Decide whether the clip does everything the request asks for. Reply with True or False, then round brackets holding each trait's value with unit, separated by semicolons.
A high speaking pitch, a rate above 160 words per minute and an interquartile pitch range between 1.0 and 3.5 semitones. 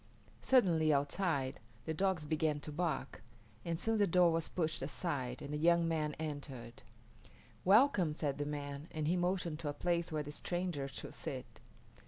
False (155 Hz; 170 wpm; 3.2 semitones)